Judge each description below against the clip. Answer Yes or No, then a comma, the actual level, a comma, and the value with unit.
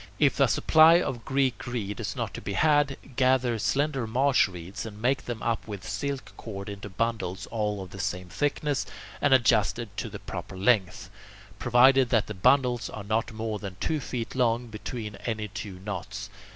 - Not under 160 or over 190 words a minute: Yes, average, 180 wpm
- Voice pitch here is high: No, low, 115 Hz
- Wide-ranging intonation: No, average, 4.2 semitones